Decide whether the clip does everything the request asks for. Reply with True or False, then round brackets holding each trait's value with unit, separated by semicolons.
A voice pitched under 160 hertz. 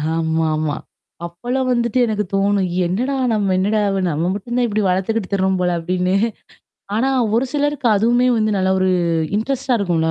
False (200 Hz)